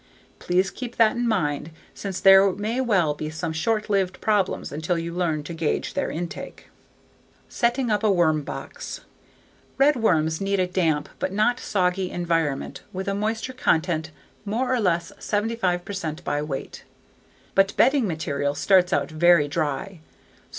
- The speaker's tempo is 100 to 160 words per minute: Yes, average, 150 wpm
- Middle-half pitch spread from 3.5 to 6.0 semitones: Yes, average, 4.8 semitones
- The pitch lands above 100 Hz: Yes, medium, 185 Hz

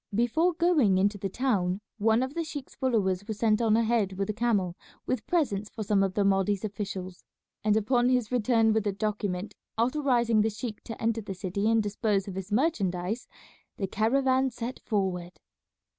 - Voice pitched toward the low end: No, high, 215 Hz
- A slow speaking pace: No, average, 180 wpm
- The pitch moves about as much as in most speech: Yes, average, 3.5 semitones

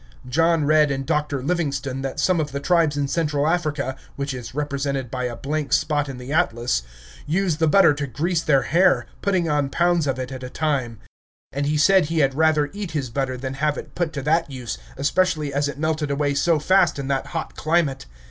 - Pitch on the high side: No, medium, 145 Hz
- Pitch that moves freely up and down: No, average, 2.8 semitones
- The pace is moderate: No, fast, 215 wpm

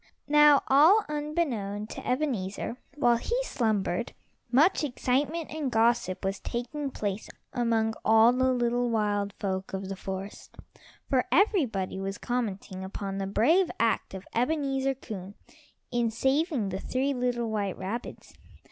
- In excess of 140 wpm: No, slow, 135 wpm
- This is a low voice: No, high, 235 Hz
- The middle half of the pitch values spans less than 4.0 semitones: No, average, 5.2 semitones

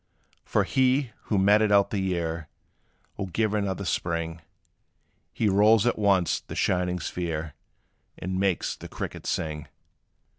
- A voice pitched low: Yes, very low, 95 Hz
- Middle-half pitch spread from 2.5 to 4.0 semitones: Yes, average, 3.5 semitones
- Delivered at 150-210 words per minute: No, slow, 135 wpm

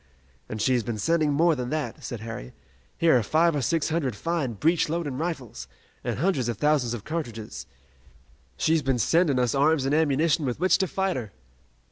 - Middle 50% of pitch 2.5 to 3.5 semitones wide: No, average, 5.2 semitones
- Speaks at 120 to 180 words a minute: No, average, 190 wpm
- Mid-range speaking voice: Yes, medium, 145 Hz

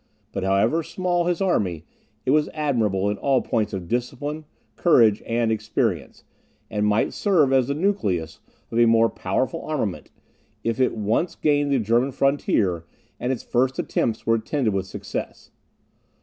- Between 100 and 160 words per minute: Yes, average, 155 wpm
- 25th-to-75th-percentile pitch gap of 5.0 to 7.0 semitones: Yes, wide, 5.5 semitones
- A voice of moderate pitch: No, low, 120 Hz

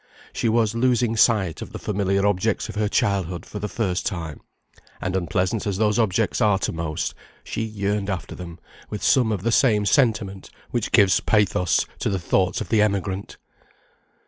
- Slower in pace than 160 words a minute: No, average, 175 wpm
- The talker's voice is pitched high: No, low, 100 Hz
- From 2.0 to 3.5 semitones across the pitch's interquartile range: Yes, average, 2.8 semitones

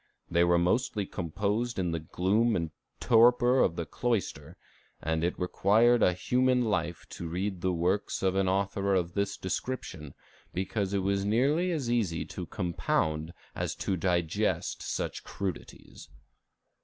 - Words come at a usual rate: Yes, average, 150 wpm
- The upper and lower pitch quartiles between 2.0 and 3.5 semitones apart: No, average, 4.7 semitones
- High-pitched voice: No, very low, 95 Hz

